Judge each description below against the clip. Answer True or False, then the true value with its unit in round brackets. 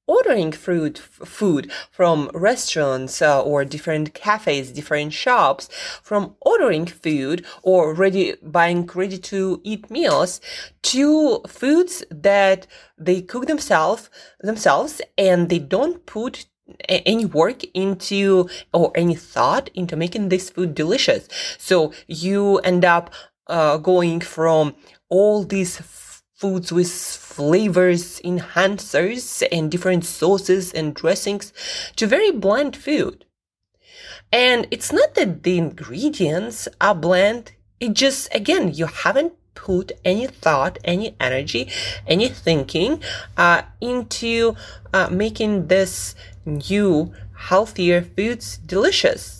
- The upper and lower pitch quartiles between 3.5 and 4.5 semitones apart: False (5.0 semitones)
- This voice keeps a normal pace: False (115 wpm)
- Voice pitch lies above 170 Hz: True (185 Hz)